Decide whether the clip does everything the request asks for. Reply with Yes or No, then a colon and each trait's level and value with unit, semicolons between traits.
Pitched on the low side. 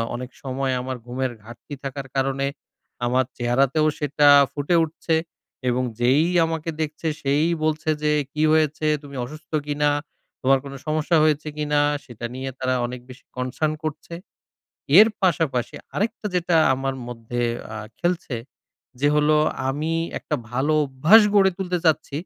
No: medium, 145 Hz